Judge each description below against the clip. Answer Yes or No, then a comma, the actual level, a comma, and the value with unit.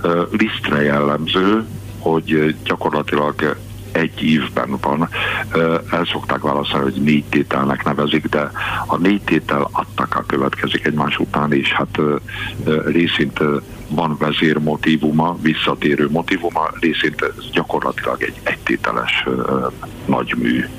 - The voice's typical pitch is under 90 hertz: Yes, very low, 80 Hz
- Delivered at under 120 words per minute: Yes, slow, 105 wpm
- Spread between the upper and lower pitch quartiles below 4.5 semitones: Yes, average, 2.8 semitones